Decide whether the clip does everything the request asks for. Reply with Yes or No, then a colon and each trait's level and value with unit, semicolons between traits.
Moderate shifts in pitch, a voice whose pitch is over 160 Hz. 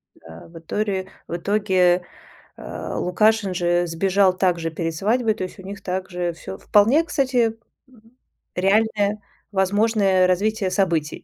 Yes: average, 3.2 semitones; high, 190 Hz